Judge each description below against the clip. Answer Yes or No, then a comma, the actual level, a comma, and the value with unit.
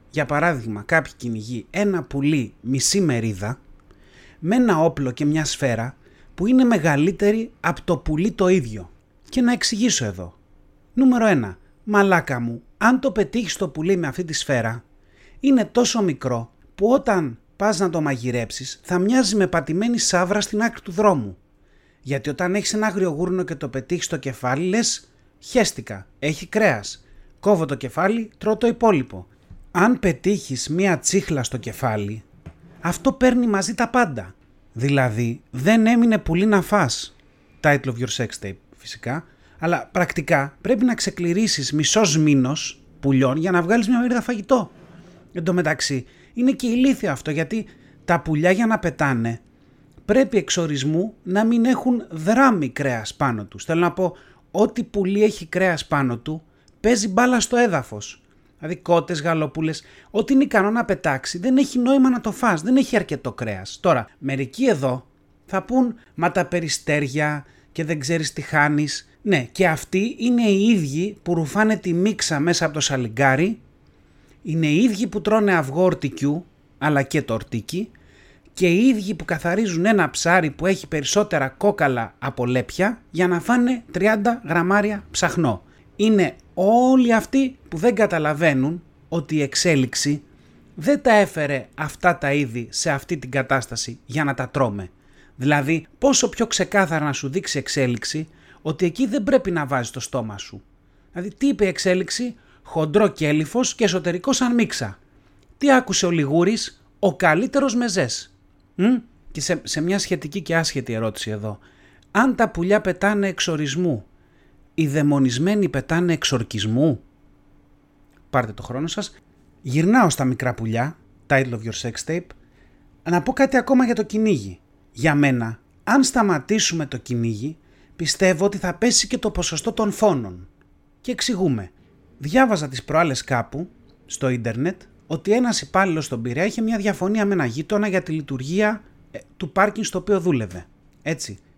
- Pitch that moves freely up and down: Yes, wide, 7.7 semitones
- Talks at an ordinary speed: Yes, average, 155 wpm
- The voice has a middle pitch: Yes, medium, 170 Hz